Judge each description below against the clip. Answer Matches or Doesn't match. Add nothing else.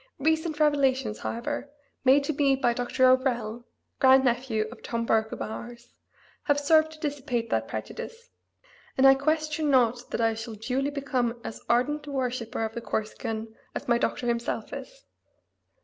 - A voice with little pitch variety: Doesn't match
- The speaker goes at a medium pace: Matches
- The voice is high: Matches